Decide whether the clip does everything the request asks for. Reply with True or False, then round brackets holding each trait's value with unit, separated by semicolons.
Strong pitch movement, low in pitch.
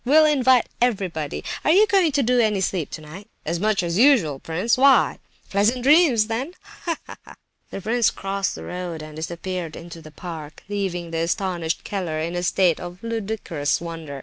False (6.1 semitones; 190 Hz)